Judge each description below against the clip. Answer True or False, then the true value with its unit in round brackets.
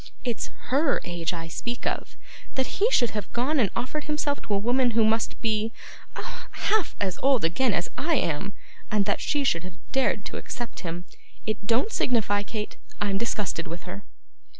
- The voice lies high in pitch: True (225 Hz)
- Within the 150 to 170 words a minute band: False (185 wpm)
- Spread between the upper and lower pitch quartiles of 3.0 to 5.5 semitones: True (5.1 semitones)